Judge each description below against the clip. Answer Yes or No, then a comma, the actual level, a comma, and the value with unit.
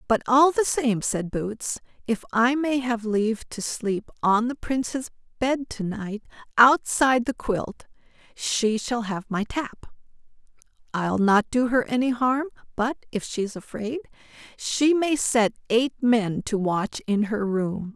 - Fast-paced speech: No, average, 155 wpm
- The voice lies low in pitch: No, high, 235 Hz